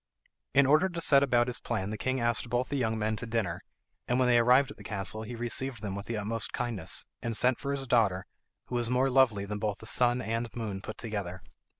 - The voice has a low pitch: Yes, low, 115 Hz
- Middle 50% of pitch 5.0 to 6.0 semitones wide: No, average, 2.9 semitones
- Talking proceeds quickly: Yes, fast, 240 wpm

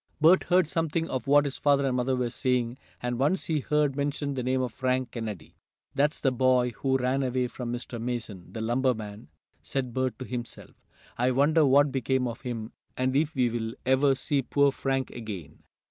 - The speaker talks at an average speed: Yes, average, 190 wpm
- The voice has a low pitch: Yes, low, 130 Hz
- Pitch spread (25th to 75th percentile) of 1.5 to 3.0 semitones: Yes, narrow, 2.5 semitones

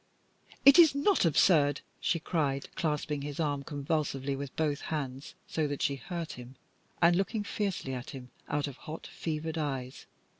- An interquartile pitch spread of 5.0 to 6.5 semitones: No, average, 3.1 semitones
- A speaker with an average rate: Yes, average, 160 wpm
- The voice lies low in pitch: No, medium, 150 Hz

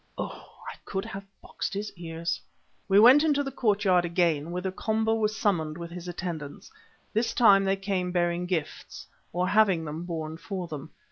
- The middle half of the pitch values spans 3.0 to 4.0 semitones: Yes, average, 3.5 semitones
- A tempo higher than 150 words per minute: Yes, average, 175 wpm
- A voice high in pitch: No, medium, 180 Hz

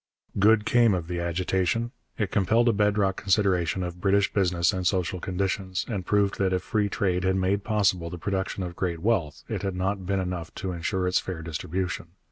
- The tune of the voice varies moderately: No, narrow, 2.1 semitones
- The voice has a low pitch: Yes, very low, 95 Hz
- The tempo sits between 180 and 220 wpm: Yes, average, 200 wpm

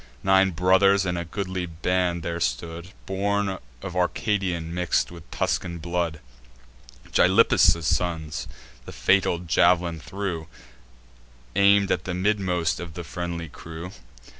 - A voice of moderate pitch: No, very low, 90 Hz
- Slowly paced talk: Yes, slow, 120 wpm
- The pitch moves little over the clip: Yes, narrow, 2.2 semitones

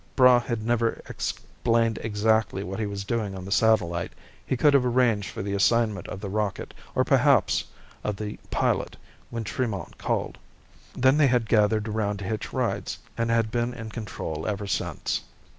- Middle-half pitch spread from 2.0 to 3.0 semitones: Yes, narrow, 2.6 semitones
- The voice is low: Yes, low, 110 Hz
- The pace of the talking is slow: No, average, 175 wpm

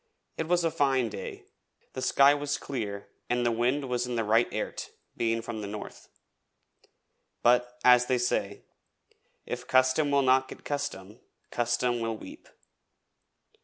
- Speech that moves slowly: No, average, 150 wpm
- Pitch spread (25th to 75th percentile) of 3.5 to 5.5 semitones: No, average, 3.1 semitones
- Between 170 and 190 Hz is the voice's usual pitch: No, low, 125 Hz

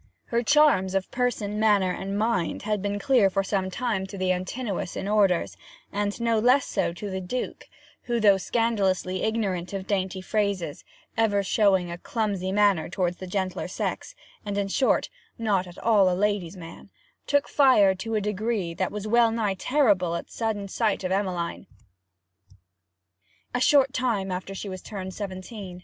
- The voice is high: Yes, high, 200 Hz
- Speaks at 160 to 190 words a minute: Yes, average, 165 wpm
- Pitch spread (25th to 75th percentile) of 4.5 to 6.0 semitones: No, average, 2.9 semitones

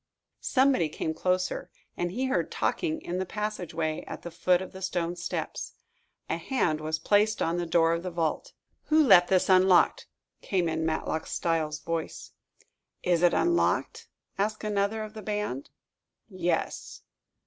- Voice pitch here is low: No, medium, 180 Hz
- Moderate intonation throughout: Yes, average, 4.2 semitones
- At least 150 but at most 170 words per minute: Yes, average, 155 wpm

